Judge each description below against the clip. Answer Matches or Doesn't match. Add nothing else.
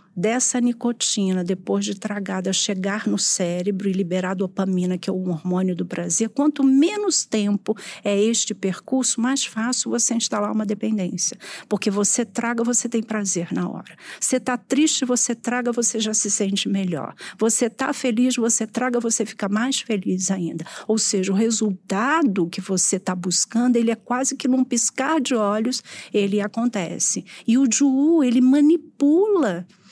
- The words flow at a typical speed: Matches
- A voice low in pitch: Doesn't match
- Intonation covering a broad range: Doesn't match